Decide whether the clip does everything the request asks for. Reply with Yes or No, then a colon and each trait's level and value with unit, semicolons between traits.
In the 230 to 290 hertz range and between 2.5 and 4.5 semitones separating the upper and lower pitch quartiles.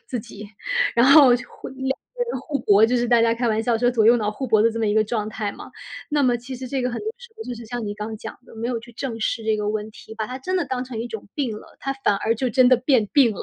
Yes: high, 235 Hz; average, 2.8 semitones